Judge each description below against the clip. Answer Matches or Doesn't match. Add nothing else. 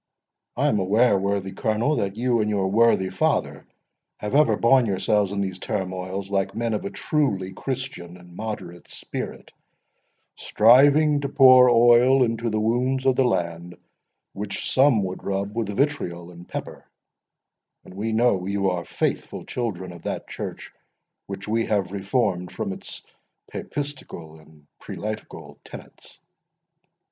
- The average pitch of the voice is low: Matches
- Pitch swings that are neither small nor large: Matches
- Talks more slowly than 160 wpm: Matches